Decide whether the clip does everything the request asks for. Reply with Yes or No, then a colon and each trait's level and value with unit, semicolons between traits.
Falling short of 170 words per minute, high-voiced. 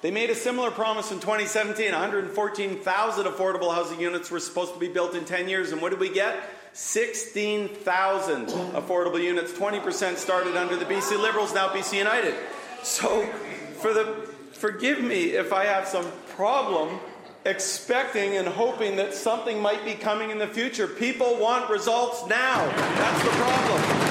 Yes: average, 160 wpm; high, 205 Hz